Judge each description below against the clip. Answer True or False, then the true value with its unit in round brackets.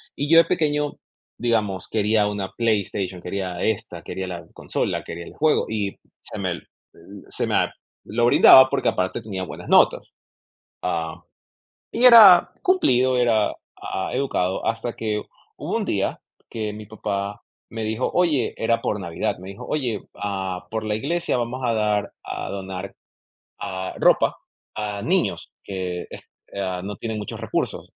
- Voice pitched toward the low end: True (105 Hz)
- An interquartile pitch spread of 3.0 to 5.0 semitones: True (3.9 semitones)